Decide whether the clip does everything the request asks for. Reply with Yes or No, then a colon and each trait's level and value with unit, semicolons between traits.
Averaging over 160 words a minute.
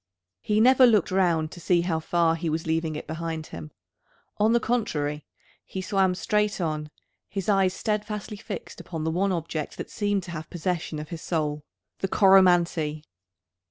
Yes: average, 170 wpm